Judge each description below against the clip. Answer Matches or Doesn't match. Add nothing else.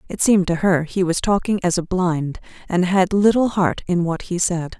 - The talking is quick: Matches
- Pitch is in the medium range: Matches